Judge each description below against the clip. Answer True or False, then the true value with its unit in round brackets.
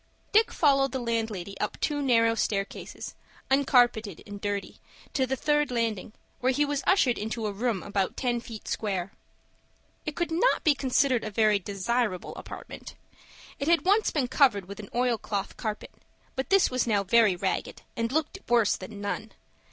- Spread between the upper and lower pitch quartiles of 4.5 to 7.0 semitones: True (5.0 semitones)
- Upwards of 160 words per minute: True (170 wpm)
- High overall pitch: True (235 Hz)